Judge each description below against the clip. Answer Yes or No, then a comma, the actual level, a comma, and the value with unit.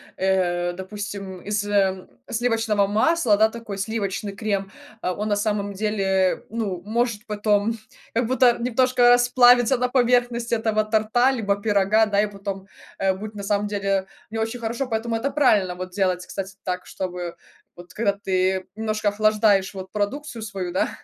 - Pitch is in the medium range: No, high, 210 Hz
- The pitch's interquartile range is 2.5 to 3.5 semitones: Yes, average, 2.8 semitones